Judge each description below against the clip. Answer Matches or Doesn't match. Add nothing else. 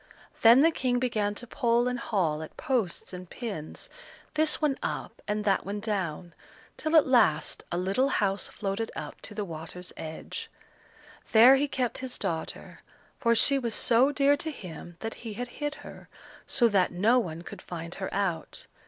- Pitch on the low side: Doesn't match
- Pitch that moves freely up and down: Matches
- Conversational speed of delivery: Matches